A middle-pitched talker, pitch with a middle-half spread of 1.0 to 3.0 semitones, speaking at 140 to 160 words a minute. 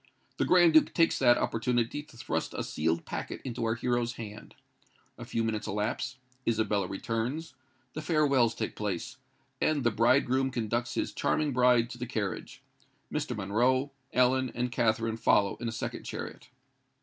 No: low, 120 Hz; average, 2.7 semitones; average, 150 wpm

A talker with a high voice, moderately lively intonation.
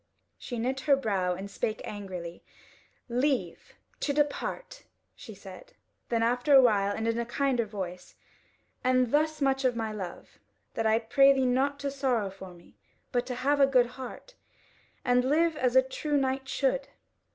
Yes: very high, 250 Hz; average, 3.9 semitones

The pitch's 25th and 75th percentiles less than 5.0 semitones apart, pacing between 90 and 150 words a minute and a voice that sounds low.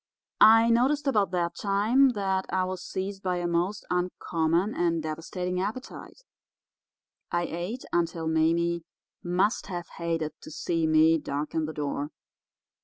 No: average, 3.3 semitones; slow, 135 wpm; medium, 175 Hz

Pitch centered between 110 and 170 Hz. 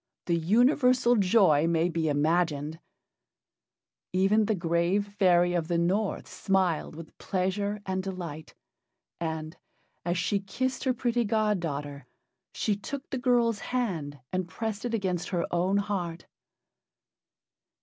No: medium, 185 Hz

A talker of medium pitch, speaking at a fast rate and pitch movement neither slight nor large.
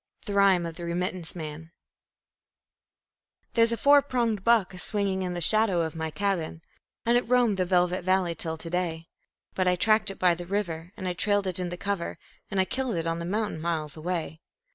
Yes: medium, 180 Hz; fast, 210 wpm; average, 3.3 semitones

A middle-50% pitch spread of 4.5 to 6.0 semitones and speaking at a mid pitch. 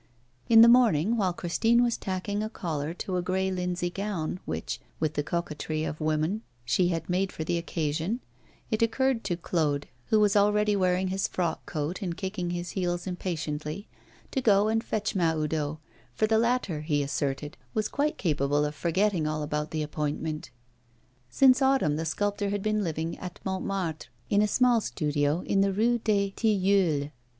Yes: average, 5.0 semitones; medium, 180 Hz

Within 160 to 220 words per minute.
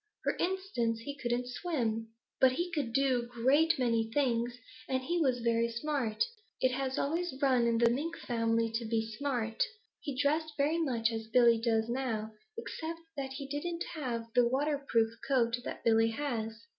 Yes: average, 170 wpm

